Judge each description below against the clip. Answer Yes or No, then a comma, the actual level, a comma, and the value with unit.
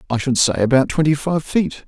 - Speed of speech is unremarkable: No, fast, 225 wpm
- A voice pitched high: No, medium, 140 Hz